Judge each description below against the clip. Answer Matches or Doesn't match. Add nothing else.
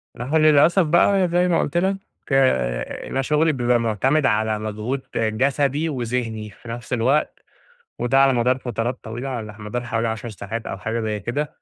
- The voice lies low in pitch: Matches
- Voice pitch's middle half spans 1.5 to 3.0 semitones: Doesn't match